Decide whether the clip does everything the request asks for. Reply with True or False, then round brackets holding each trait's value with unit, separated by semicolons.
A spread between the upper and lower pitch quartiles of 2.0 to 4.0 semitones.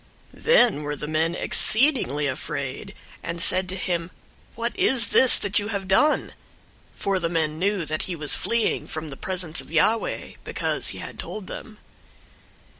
False (5.3 semitones)